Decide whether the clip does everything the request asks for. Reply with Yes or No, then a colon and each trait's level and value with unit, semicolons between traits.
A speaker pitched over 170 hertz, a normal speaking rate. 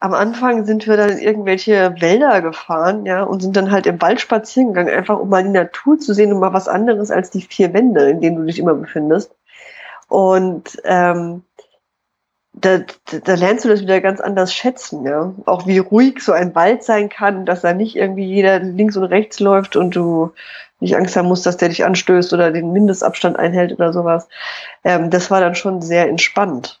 No: high, 190 Hz; fast, 210 wpm